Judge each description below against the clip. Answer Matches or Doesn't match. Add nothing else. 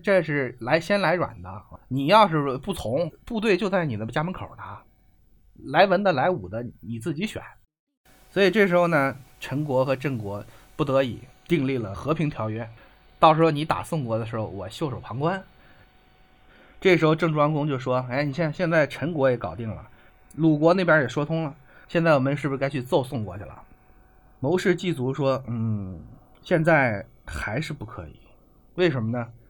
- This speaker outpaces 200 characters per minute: Matches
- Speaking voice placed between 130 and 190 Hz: Matches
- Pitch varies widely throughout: Matches